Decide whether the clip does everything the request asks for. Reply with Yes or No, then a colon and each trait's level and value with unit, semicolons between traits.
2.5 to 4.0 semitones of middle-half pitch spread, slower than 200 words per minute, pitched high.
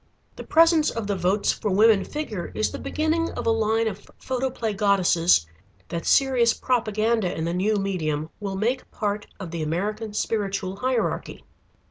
Yes: average, 3.5 semitones; average, 160 wpm; high, 210 Hz